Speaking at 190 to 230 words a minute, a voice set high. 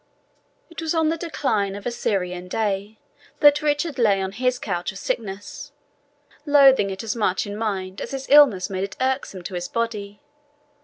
No: average, 175 wpm; high, 215 Hz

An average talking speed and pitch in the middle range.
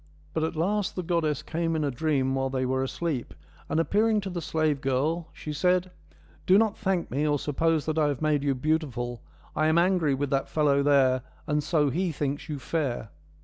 No: fast, 210 wpm; medium, 155 Hz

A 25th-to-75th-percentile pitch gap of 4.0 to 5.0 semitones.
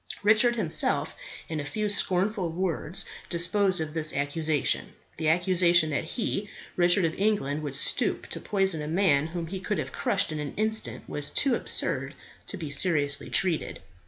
Yes: average, 4.3 semitones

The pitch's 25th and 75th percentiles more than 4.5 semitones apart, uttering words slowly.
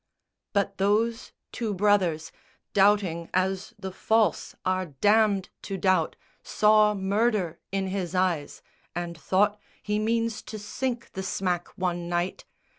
No: narrow, 2.6 semitones; slow, 125 wpm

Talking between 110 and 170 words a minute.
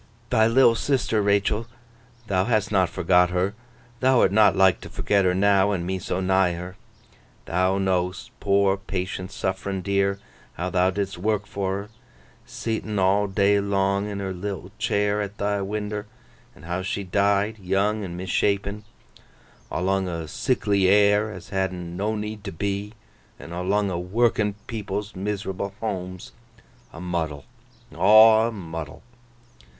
Yes: average, 145 wpm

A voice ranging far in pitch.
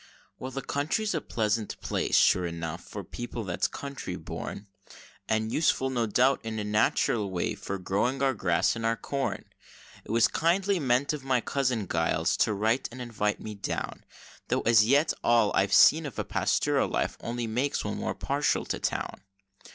No: average, 4.4 semitones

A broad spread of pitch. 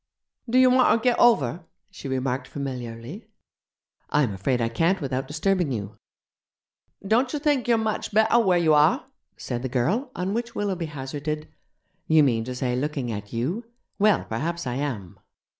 Yes: wide, 8.5 semitones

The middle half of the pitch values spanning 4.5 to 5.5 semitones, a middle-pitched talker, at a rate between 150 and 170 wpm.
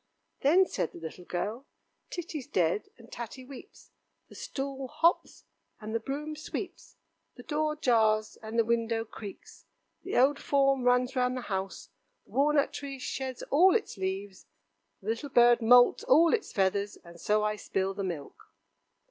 No: average, 4.8 semitones; high, 240 Hz; average, 160 wpm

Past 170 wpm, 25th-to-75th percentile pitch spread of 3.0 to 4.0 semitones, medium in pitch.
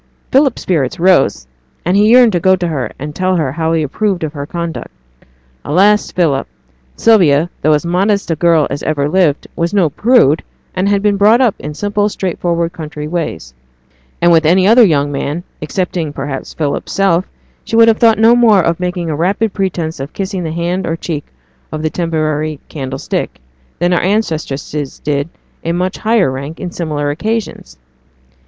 No: average, 180 wpm; average, 4.4 semitones; medium, 170 Hz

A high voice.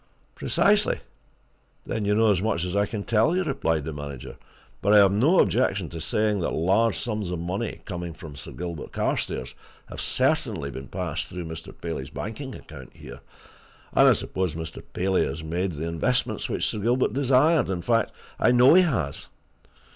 No: very low, 95 Hz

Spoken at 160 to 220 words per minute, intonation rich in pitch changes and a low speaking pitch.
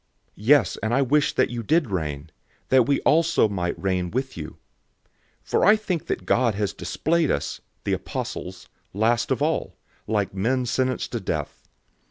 Yes: average, 170 wpm; wide, 6.3 semitones; low, 115 Hz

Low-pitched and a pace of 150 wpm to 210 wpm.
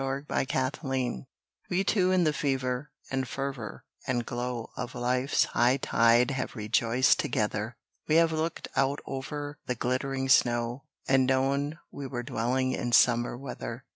No: low, 130 Hz; average, 140 wpm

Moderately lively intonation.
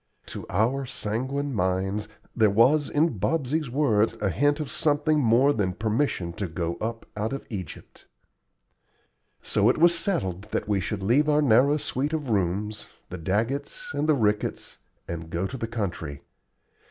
No: wide, 6.5 semitones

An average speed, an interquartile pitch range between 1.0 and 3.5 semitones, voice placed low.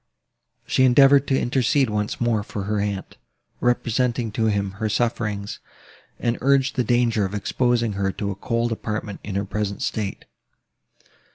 Yes: average, 155 wpm; average, 3.1 semitones; low, 110 Hz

